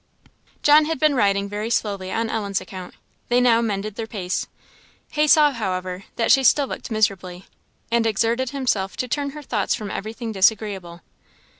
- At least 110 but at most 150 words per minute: No, average, 165 wpm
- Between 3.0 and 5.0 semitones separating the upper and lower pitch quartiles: Yes, average, 4.2 semitones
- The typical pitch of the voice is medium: No, high, 220 Hz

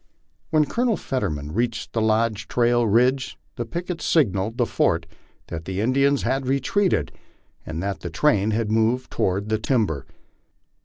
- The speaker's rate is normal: Yes, average, 145 wpm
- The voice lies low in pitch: Yes, low, 115 Hz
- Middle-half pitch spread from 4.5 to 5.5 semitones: Yes, average, 5.0 semitones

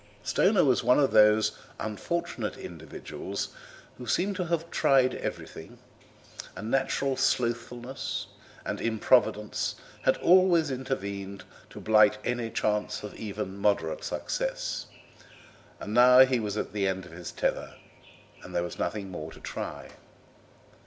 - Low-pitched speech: Yes, low, 115 Hz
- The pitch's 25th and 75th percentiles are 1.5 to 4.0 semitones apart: No, average, 4.6 semitones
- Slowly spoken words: Yes, slow, 130 wpm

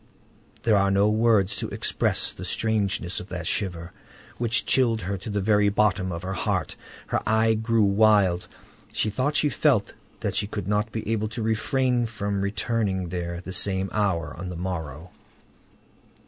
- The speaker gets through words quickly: No, average, 175 wpm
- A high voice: No, low, 100 Hz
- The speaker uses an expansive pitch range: No, average, 3.1 semitones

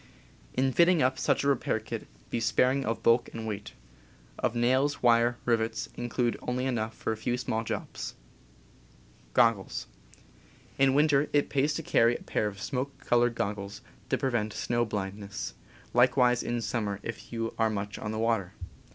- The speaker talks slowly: No, average, 170 wpm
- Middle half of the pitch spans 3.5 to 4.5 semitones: No, average, 2.8 semitones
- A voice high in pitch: No, low, 120 Hz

